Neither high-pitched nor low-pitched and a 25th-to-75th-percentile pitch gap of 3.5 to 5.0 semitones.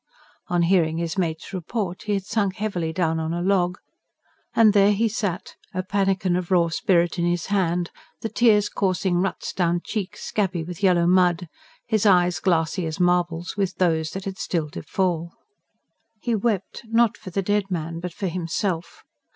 No: medium, 180 Hz; narrow, 2.6 semitones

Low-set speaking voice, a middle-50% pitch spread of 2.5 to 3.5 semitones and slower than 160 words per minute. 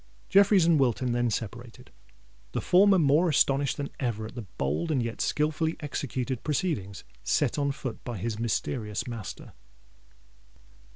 No: low, 130 Hz; average, 4.8 semitones; average, 140 wpm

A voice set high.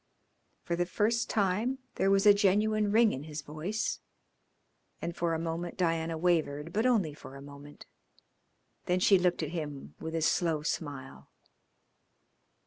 No: medium, 170 Hz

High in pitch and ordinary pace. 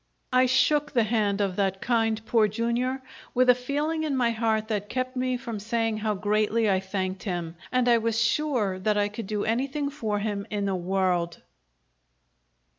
Yes: high, 220 Hz; average, 185 wpm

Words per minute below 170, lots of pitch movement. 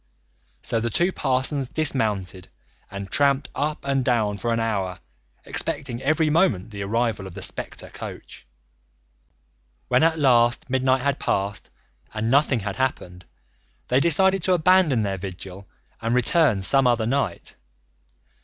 Yes: average, 140 wpm; wide, 5.7 semitones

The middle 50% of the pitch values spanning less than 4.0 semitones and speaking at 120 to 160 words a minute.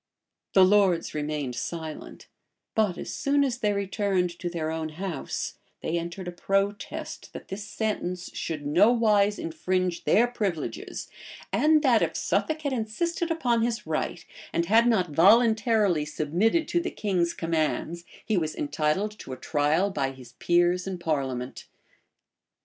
No: average, 5.3 semitones; average, 145 wpm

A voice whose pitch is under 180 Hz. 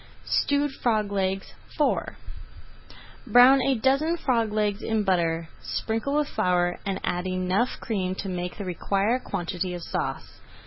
No: high, 200 Hz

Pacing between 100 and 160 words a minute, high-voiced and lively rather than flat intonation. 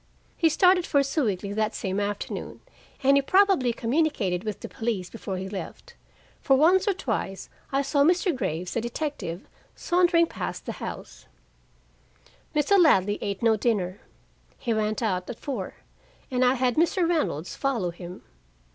Yes: average, 155 wpm; high, 240 Hz; wide, 7.8 semitones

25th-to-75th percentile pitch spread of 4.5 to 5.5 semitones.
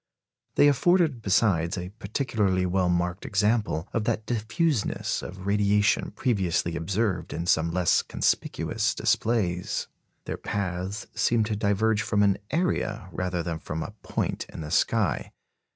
No: average, 3.8 semitones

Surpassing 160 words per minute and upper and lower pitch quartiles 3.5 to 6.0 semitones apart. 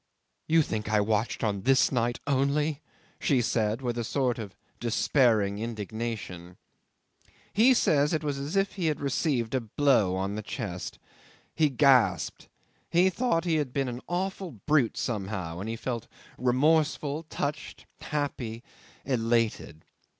No: average, 145 wpm; average, 5.2 semitones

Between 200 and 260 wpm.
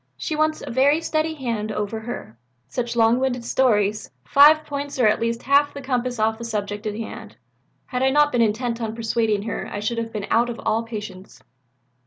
Yes: fast, 205 wpm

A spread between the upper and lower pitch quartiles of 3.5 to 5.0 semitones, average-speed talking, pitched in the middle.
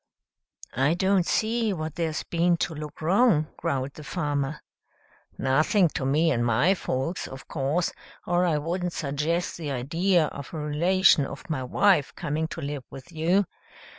Yes: average, 3.8 semitones; average, 160 wpm; medium, 160 Hz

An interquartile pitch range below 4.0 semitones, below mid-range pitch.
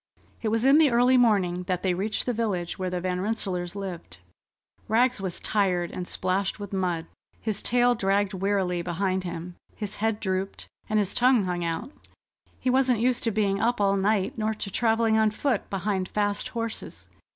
No: average, 3.4 semitones; high, 200 Hz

